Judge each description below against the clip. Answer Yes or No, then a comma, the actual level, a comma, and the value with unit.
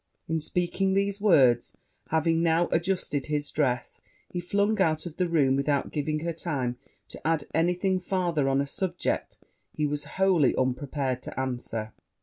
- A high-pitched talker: No, medium, 155 Hz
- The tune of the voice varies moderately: Yes, average, 4.3 semitones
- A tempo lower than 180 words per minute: Yes, average, 160 wpm